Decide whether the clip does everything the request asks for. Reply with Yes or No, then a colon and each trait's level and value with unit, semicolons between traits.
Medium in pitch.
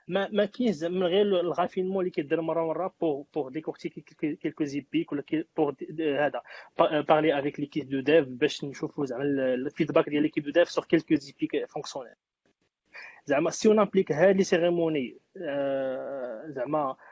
Yes: medium, 160 Hz